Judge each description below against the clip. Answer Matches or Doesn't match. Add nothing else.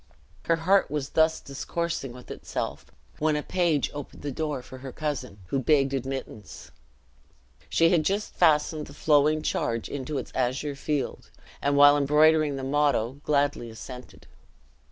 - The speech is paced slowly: Doesn't match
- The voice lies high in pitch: Doesn't match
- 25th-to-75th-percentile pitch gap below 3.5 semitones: Matches